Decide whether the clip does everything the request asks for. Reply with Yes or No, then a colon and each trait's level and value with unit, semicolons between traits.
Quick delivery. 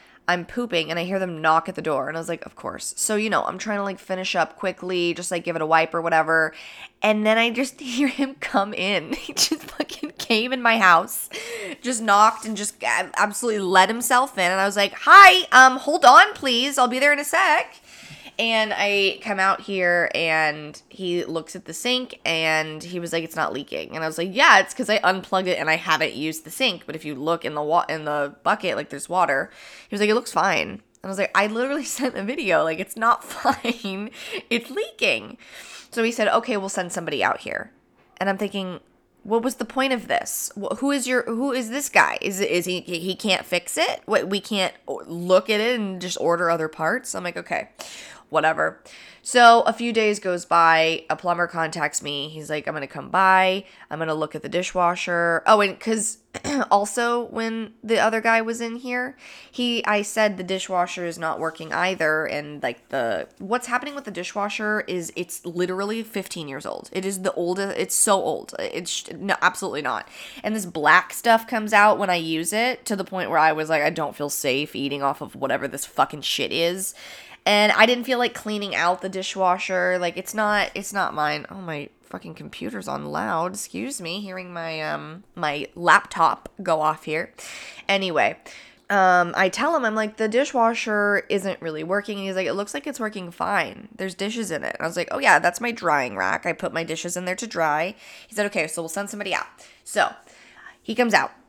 Yes: fast, 220 wpm